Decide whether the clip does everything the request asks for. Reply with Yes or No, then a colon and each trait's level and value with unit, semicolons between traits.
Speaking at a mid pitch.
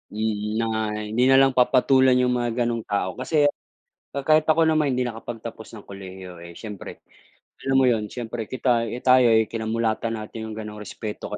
No: low, 115 Hz